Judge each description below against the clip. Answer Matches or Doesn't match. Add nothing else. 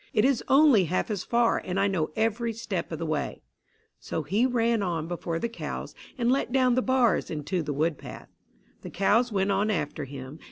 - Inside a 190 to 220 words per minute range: Matches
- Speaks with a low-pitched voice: Doesn't match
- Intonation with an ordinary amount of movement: Doesn't match